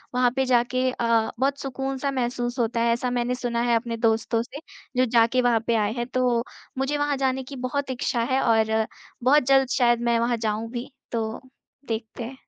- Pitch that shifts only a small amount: Yes, narrow, 2.0 semitones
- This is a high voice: Yes, high, 245 Hz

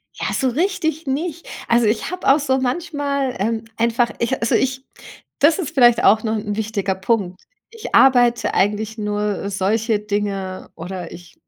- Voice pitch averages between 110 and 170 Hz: No, high, 230 Hz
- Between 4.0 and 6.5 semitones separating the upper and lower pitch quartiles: Yes, average, 4.5 semitones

